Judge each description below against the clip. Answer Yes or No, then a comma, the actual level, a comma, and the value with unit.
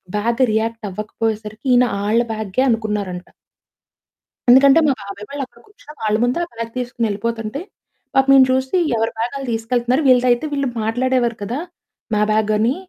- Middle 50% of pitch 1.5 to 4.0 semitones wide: Yes, average, 3.1 semitones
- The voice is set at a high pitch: Yes, high, 230 Hz